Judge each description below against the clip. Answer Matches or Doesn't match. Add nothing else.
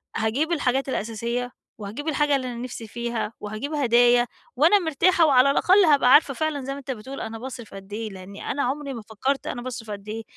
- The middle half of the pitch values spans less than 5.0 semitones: Matches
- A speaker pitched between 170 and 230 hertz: Doesn't match